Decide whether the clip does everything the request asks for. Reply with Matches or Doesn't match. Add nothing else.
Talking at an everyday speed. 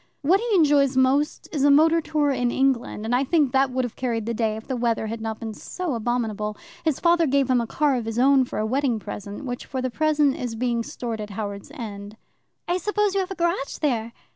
Doesn't match